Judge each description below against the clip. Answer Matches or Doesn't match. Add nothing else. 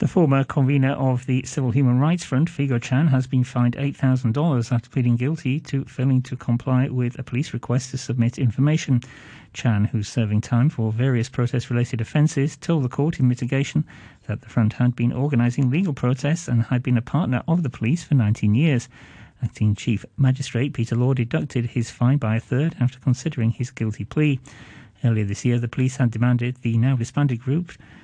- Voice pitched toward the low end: Matches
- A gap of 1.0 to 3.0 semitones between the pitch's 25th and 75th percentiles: Matches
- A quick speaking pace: Doesn't match